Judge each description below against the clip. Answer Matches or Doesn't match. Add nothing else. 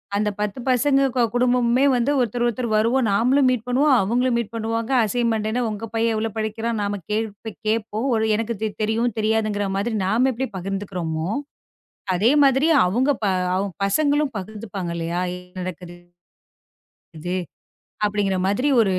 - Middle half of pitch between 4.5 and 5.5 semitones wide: Doesn't match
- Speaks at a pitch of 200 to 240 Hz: Matches